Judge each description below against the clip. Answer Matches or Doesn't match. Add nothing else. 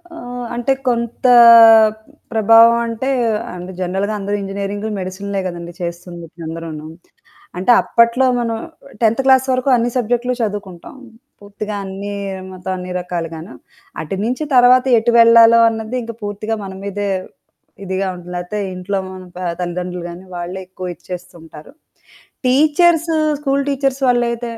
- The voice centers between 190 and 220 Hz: Matches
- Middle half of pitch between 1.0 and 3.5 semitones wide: Doesn't match